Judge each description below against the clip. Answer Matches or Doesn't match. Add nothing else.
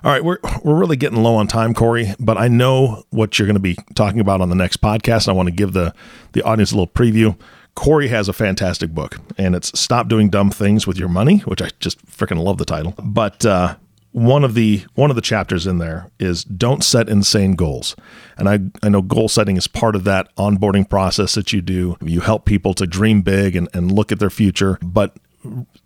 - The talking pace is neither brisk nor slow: Doesn't match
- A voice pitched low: Matches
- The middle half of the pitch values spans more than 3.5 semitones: Doesn't match